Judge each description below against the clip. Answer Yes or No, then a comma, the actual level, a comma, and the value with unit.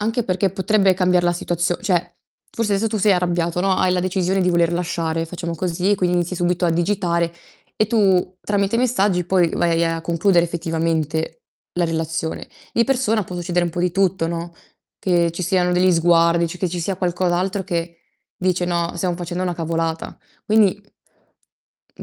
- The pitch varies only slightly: Yes, narrow, 2.1 semitones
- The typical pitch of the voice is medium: Yes, medium, 175 Hz